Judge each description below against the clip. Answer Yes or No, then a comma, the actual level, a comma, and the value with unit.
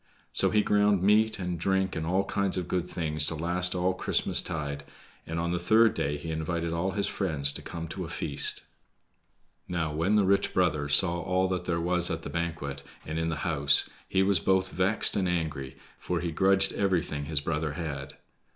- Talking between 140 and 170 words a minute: No, average, 195 wpm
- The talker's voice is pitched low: Yes, very low, 85 Hz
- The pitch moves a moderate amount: Yes, average, 3.1 semitones